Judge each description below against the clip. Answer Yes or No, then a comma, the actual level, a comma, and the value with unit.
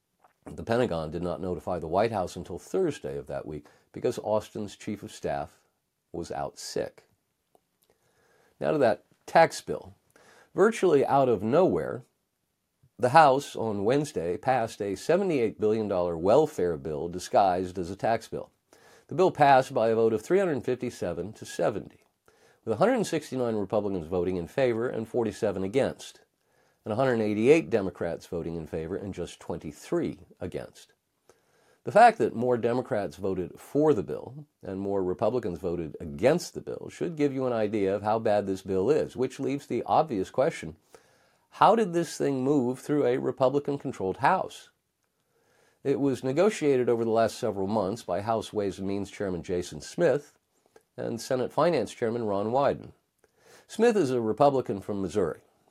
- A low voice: Yes, low, 110 Hz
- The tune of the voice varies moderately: No, wide, 5.7 semitones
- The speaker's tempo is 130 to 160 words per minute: Yes, average, 155 wpm